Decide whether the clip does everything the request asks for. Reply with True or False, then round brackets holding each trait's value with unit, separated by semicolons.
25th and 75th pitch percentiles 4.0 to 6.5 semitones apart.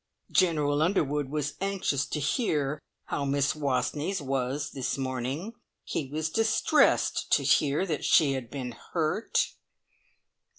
False (2.9 semitones)